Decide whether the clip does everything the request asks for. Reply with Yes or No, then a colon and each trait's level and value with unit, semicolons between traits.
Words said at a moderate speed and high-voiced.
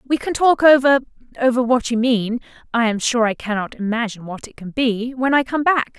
No: fast, 210 wpm; high, 245 Hz